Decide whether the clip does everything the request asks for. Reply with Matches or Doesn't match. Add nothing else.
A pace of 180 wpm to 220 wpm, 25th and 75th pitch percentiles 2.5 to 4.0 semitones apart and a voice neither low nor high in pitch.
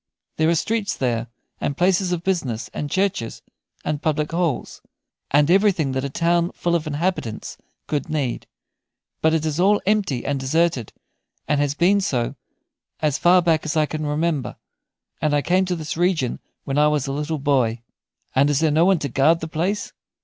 Matches